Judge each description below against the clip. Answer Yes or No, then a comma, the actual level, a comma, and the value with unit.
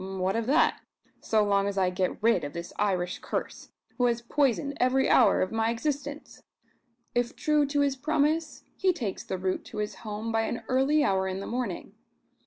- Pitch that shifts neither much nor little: No, wide, 6.5 semitones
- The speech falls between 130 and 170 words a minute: No, average, 195 wpm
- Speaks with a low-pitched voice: No, high, 230 Hz